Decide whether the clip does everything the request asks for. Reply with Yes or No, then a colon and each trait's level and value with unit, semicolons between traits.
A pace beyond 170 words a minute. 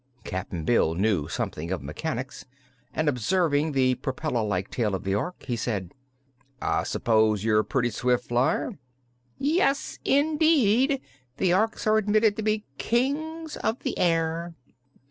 No: average, 145 wpm